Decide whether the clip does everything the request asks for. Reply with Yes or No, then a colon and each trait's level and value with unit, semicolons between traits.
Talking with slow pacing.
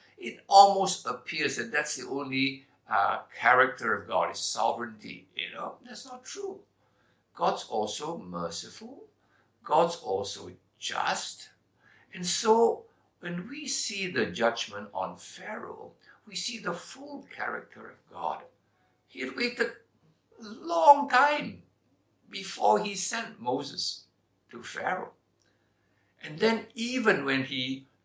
Yes: slow, 120 wpm